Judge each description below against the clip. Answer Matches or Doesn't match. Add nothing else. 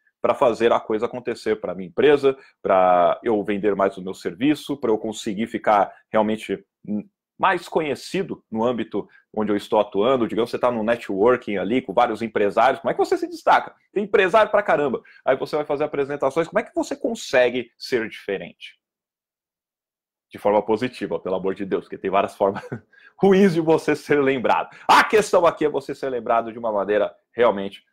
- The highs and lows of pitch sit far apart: Matches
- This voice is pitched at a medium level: Doesn't match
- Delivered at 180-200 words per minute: Matches